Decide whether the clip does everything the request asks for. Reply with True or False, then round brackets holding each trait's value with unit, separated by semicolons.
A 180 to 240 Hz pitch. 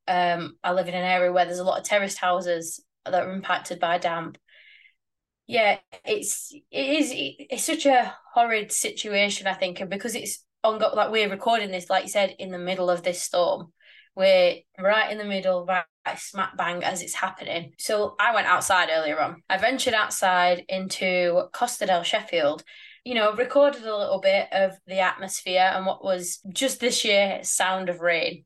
True (190 Hz)